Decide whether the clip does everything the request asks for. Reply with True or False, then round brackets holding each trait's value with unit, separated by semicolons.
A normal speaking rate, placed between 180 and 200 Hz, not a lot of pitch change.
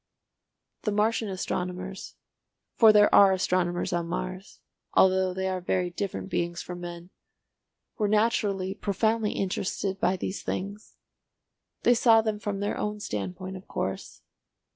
False (125 wpm; 190 Hz; 2.3 semitones)